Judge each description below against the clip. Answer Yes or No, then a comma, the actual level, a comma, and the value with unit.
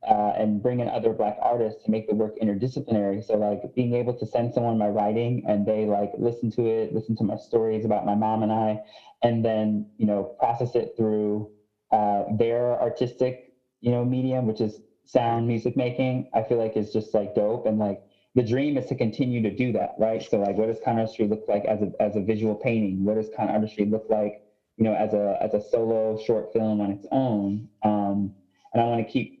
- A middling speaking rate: No, fast, 220 wpm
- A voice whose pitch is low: Yes, low, 110 Hz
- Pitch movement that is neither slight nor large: No, narrow, 2.1 semitones